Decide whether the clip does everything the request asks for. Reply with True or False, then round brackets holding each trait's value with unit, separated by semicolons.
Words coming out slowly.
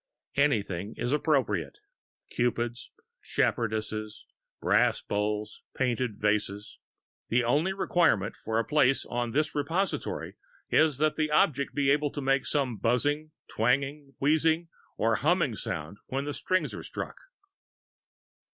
True (125 wpm)